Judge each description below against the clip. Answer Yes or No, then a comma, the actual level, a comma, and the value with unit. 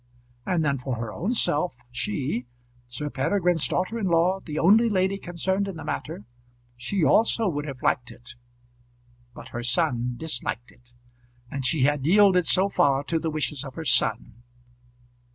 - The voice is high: No, medium, 155 Hz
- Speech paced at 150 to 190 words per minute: Yes, average, 165 wpm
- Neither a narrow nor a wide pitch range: No, wide, 6.5 semitones